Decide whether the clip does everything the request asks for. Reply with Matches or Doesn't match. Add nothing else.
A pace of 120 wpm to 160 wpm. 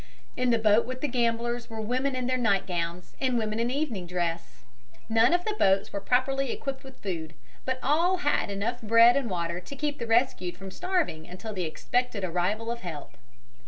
Doesn't match